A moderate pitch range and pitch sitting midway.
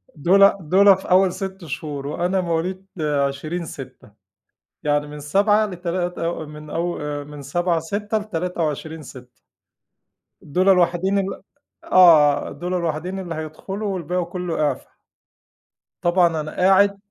Yes: average, 3.8 semitones; medium, 175 Hz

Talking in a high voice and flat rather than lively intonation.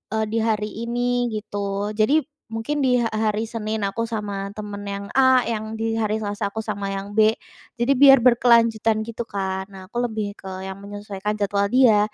Yes: high, 215 Hz; narrow, 2.3 semitones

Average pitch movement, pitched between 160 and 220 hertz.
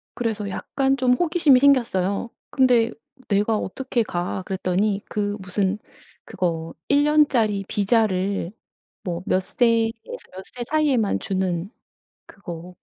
Yes: average, 4.8 semitones; high, 210 Hz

